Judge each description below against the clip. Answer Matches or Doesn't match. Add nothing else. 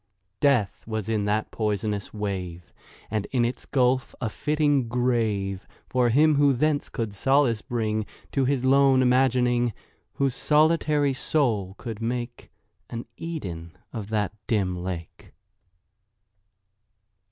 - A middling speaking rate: Doesn't match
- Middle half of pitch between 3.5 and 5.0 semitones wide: Matches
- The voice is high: Doesn't match